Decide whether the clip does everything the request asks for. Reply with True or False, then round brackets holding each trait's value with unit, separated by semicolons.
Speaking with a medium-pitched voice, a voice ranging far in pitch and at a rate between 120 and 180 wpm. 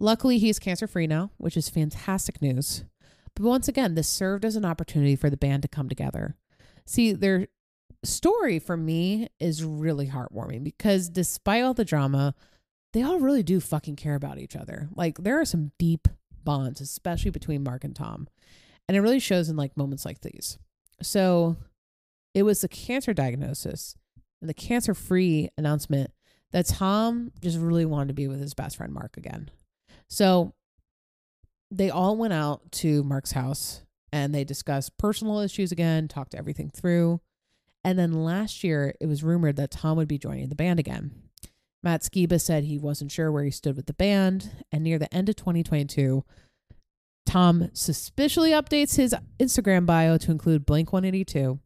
False (165 Hz; 5.0 semitones; 170 wpm)